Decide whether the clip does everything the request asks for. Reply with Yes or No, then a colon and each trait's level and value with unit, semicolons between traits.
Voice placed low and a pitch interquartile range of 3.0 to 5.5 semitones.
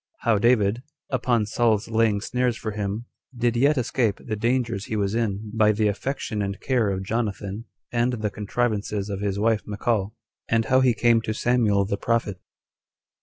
No: low, 110 Hz; narrow, 2.6 semitones